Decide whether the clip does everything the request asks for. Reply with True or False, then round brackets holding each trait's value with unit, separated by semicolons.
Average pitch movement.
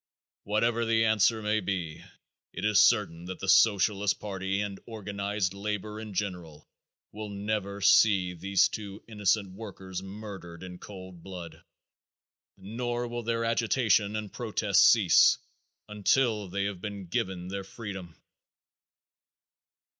False (2.3 semitones)